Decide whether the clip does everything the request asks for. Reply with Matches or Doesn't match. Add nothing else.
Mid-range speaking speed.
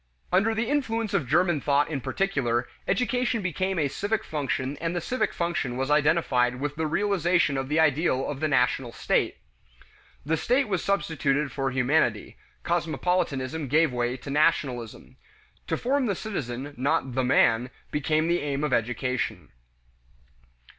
Matches